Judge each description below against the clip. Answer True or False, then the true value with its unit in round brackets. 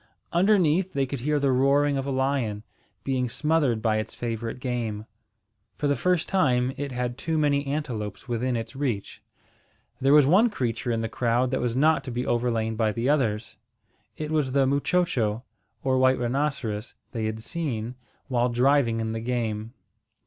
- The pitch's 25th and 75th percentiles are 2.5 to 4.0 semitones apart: True (3.7 semitones)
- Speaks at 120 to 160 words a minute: False (170 wpm)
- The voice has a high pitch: False (125 Hz)